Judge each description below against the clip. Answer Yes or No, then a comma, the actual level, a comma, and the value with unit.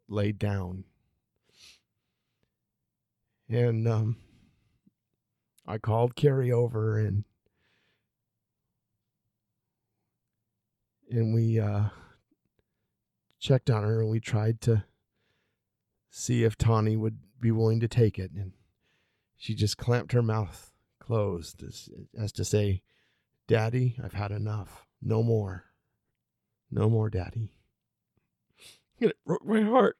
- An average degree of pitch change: No, narrow, 1.9 semitones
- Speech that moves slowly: Yes, slow, 105 wpm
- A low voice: Yes, low, 110 Hz